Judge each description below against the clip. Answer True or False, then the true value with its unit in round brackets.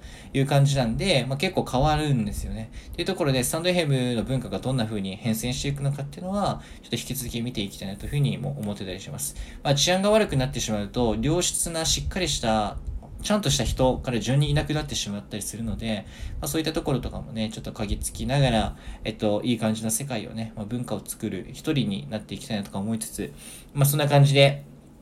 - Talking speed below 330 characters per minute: False (490 characters per minute)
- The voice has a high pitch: False (120 Hz)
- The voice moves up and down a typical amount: True (4.8 semitones)